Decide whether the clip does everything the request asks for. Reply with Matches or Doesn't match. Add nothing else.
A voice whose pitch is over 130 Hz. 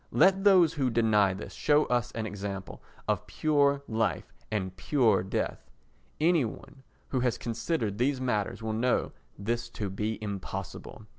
Doesn't match